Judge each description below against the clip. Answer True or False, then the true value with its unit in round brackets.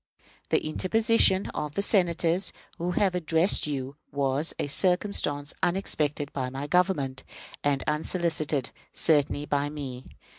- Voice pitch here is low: False (150 Hz)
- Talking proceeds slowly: True (120 wpm)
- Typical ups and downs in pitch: True (4.0 semitones)